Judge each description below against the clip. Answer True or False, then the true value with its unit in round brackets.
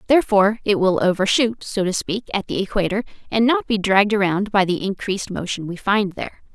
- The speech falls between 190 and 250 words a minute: True (200 wpm)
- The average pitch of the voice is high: True (200 Hz)